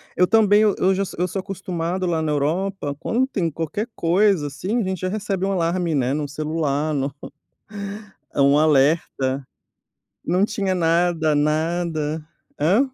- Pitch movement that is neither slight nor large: Yes, average, 4.1 semitones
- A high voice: No, medium, 170 Hz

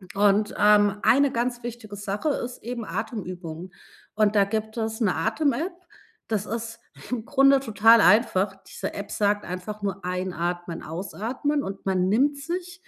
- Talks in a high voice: Yes, high, 215 Hz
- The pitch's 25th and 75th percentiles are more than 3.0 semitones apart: Yes, average, 3.6 semitones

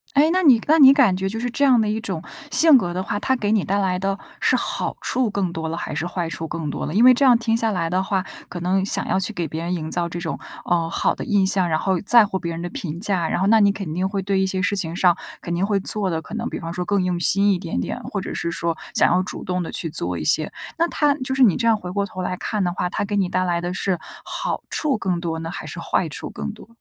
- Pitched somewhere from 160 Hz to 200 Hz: Yes, high, 190 Hz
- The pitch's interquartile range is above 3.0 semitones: Yes, average, 3.7 semitones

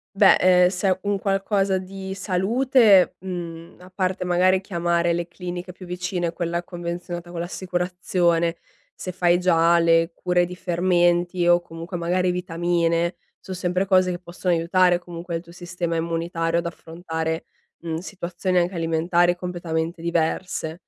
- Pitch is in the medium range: Yes, medium, 175 Hz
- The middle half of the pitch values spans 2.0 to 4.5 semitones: No, narrow, 1.4 semitones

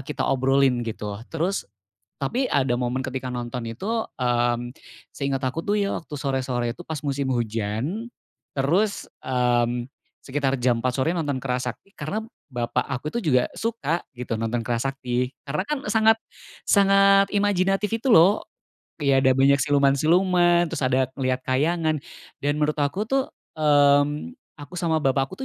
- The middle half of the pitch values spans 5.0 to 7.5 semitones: Yes, wide, 5.5 semitones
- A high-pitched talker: No, medium, 140 Hz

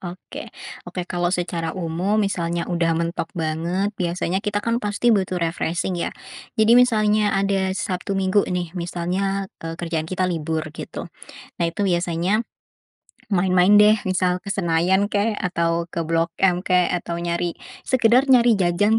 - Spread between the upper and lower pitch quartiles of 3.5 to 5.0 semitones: No, average, 2.9 semitones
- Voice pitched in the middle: Yes, medium, 180 Hz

